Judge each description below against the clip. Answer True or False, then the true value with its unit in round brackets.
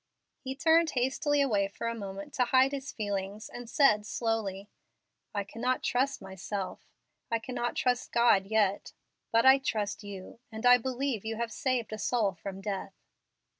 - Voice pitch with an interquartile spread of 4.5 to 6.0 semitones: False (4.1 semitones)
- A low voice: False (225 Hz)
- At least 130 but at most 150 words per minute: False (165 wpm)